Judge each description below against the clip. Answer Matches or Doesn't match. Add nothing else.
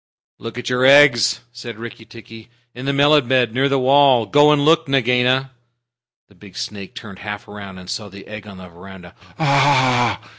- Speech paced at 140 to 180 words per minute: Doesn't match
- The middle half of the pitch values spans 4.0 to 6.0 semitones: Matches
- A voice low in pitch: Matches